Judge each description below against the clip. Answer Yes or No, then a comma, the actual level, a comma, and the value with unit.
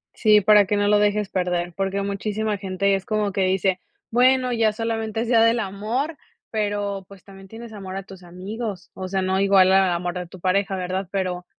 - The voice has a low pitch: No, high, 200 Hz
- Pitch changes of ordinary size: No, narrow, 2.2 semitones